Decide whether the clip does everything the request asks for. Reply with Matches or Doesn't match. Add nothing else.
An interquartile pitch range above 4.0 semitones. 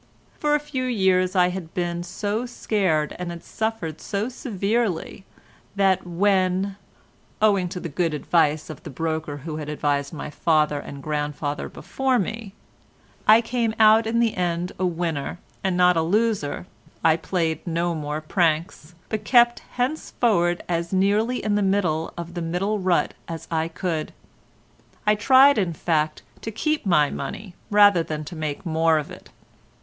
Matches